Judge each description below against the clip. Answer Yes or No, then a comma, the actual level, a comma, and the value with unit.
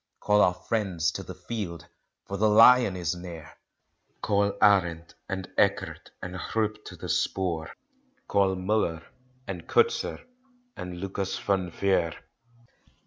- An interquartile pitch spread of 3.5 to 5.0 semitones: No, average, 2.9 semitones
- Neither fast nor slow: No, slow, 130 wpm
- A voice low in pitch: Yes, very low, 95 Hz